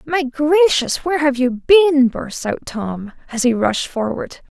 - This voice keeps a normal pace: Yes, average, 170 wpm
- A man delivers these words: No, female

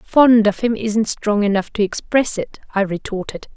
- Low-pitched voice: No, high, 215 Hz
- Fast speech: No, average, 185 wpm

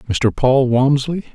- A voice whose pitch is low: Yes, low, 130 Hz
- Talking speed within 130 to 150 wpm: Yes, slow, 135 wpm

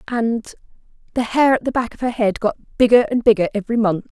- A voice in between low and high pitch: No, high, 230 Hz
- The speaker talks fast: Yes, fast, 215 wpm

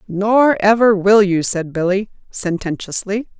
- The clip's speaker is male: No, female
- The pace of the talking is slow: Yes, slow, 125 wpm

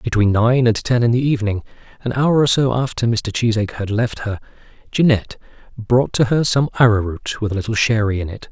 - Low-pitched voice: Yes, low, 115 Hz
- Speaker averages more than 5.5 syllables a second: Yes, 5.8 syllables/s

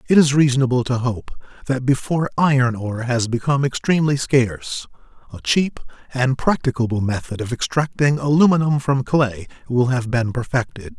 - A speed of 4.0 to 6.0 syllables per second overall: Yes, 5.4 syllables/s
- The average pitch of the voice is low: Yes, low, 130 Hz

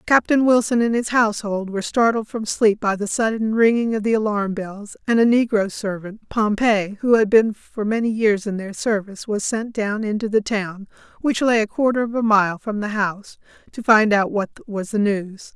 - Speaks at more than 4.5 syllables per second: Yes, 5.0 syllables/s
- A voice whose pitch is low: No, high, 215 Hz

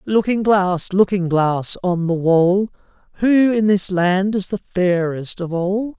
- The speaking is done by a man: Yes, male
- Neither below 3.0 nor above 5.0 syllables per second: Yes, 3.6 syllables/s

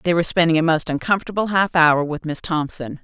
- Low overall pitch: No, medium, 165 Hz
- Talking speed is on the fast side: Yes, fast, 220 wpm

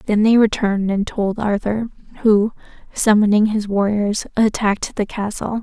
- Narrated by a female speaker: Yes, female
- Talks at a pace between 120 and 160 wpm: Yes, average, 140 wpm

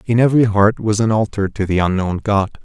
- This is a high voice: No, low, 105 Hz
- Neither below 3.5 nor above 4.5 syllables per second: No, 5.9 syllables/s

